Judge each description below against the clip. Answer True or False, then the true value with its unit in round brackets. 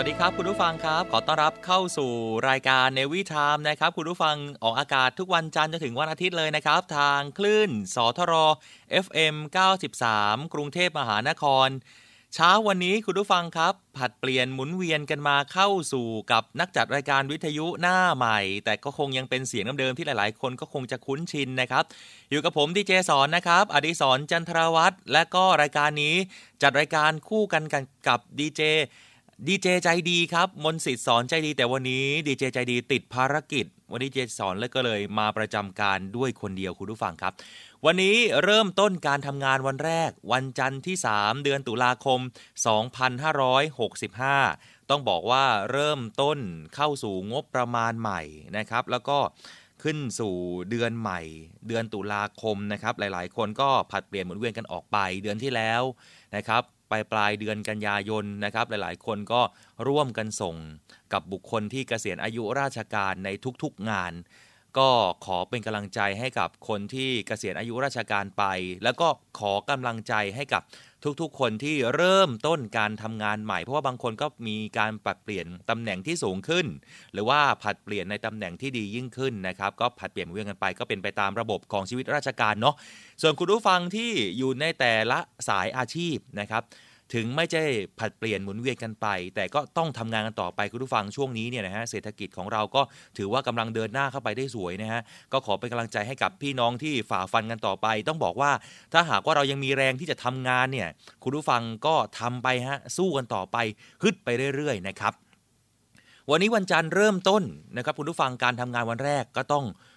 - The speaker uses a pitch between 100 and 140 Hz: True (130 Hz)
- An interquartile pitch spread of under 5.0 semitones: False (5.6 semitones)